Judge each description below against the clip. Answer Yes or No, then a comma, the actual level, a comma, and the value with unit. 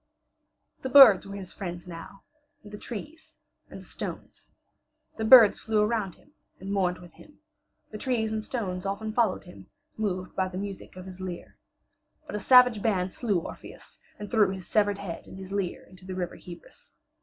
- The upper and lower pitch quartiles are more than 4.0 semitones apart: No, average, 3.0 semitones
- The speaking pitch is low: No, high, 200 Hz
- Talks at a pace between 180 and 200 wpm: Yes, average, 185 wpm